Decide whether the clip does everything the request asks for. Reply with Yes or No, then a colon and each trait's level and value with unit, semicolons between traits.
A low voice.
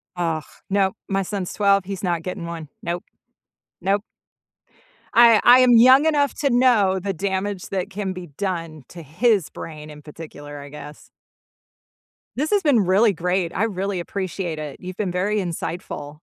No: high, 190 Hz